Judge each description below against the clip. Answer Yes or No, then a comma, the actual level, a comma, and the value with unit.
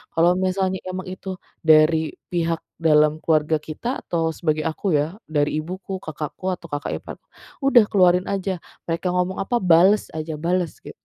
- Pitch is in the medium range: Yes, medium, 170 Hz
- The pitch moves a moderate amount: Yes, average, 3.1 semitones